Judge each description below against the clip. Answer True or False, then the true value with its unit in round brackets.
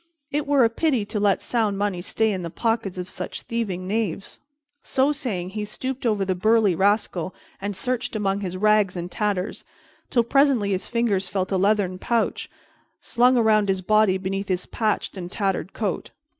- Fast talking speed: False (180 wpm)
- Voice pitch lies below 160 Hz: False (205 Hz)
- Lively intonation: False (3.3 semitones)